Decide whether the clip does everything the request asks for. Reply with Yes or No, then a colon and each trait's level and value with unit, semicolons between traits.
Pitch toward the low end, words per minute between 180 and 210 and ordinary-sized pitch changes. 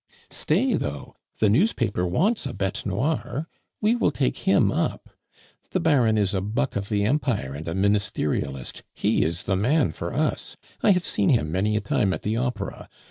No: low, 105 Hz; average, 185 wpm; wide, 7.3 semitones